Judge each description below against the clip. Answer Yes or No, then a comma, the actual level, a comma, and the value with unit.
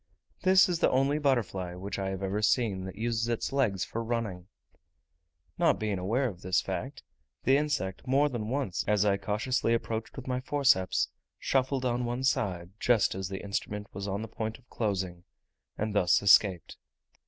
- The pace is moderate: Yes, average, 175 wpm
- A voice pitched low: Yes, low, 110 Hz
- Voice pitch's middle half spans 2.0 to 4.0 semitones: No, average, 4.9 semitones